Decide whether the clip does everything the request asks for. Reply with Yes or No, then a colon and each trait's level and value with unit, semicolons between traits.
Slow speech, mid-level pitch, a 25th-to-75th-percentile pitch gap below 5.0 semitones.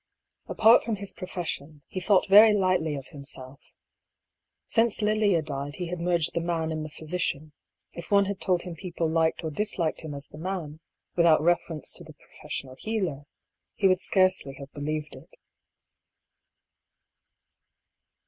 No: average, 155 wpm; medium, 170 Hz; average, 3.8 semitones